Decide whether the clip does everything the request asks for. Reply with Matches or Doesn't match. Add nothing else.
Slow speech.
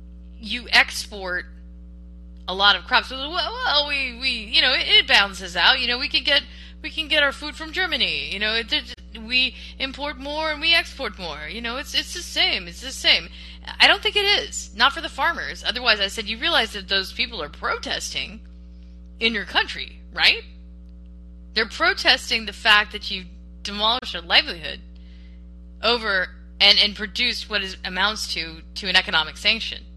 Doesn't match